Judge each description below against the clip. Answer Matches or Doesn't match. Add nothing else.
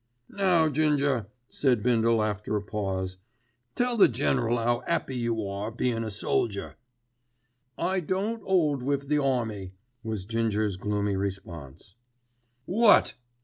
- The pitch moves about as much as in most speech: Doesn't match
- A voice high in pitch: Doesn't match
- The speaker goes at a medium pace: Doesn't match